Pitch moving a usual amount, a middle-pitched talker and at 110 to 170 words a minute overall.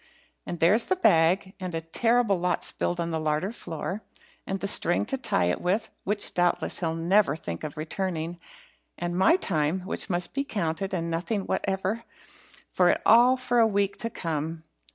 No: average, 4.0 semitones; medium, 180 Hz; average, 180 wpm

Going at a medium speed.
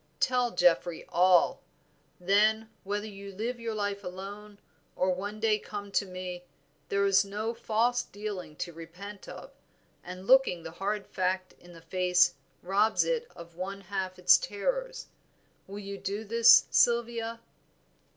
Yes: average, 145 wpm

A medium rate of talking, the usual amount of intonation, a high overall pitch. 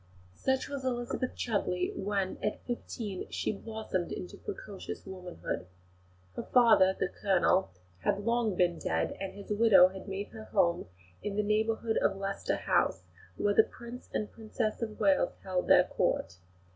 Yes: average, 155 wpm; average, 3.1 semitones; high, 205 Hz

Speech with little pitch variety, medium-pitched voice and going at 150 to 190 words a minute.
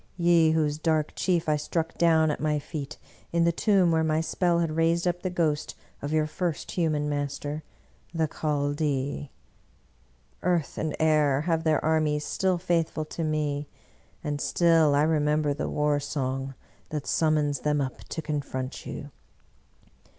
Yes: narrow, 1.9 semitones; medium, 155 Hz; average, 160 wpm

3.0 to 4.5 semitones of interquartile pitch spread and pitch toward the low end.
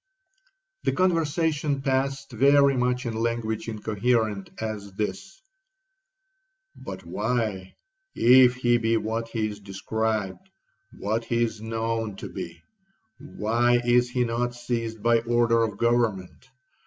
Yes: average, 3.7 semitones; low, 120 Hz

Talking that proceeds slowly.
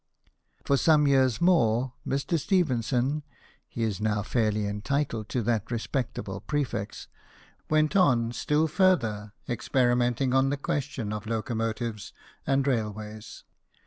Yes: slow, 115 wpm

